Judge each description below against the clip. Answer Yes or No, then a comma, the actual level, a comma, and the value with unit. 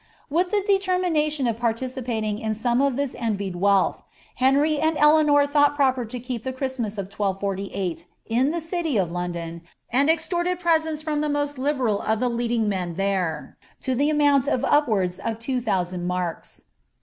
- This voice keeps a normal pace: Yes, average, 175 wpm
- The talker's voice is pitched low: No, very high, 250 Hz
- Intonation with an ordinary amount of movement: No, wide, 6.7 semitones